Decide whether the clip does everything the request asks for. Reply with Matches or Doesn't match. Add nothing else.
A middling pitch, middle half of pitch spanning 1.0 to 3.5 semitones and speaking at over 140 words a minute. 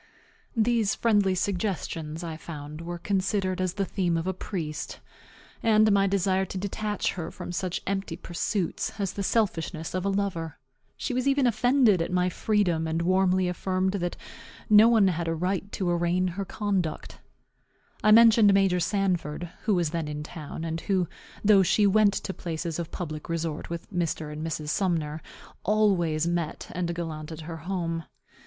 Matches